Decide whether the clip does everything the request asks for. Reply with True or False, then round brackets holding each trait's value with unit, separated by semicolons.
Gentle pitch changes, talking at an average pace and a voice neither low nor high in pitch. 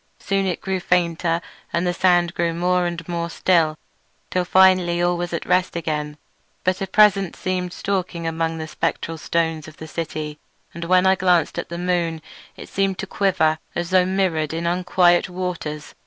True (1.9 semitones; 180 wpm; 175 Hz)